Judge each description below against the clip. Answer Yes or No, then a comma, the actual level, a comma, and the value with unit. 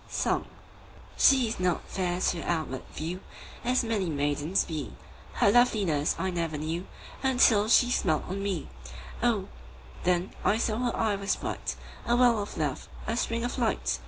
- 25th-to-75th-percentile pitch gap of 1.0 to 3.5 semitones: No, wide, 5.5 semitones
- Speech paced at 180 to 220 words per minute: No, average, 165 wpm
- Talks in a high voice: Yes, high, 195 Hz